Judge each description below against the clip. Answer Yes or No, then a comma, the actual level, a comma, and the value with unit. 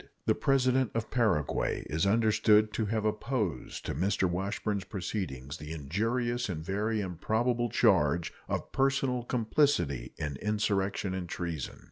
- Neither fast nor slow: No, slow, 130 wpm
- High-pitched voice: No, low, 105 Hz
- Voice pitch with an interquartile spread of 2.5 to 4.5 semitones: No, average, 5.1 semitones